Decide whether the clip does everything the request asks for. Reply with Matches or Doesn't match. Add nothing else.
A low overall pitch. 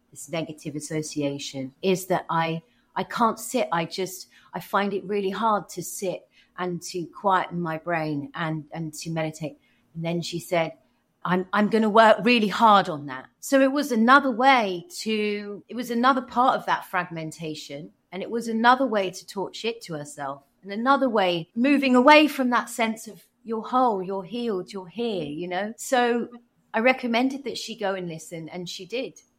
Doesn't match